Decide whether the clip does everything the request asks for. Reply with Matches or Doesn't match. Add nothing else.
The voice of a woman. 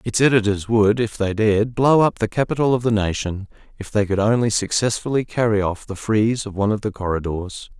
Doesn't match